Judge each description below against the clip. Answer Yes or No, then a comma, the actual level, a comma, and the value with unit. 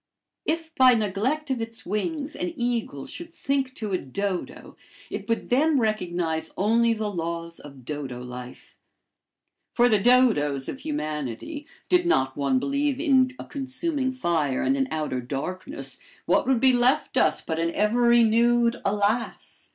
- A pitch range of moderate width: No, wide, 7.9 semitones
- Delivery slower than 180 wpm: Yes, average, 150 wpm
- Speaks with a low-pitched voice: No, high, 225 Hz